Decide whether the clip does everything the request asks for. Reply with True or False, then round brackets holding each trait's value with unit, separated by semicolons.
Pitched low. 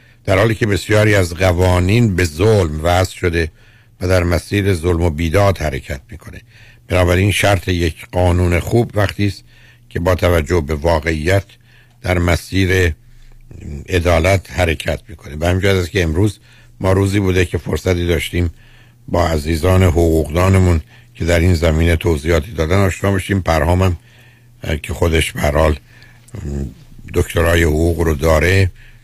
True (90 Hz)